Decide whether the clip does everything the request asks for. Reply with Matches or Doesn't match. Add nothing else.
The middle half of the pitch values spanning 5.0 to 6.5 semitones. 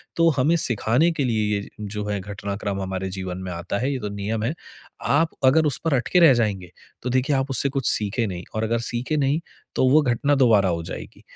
Matches